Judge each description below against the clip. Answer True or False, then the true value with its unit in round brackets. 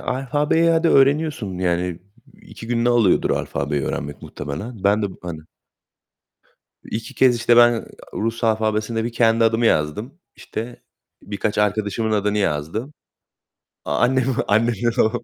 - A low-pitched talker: True (110 Hz)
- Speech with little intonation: False (3.1 semitones)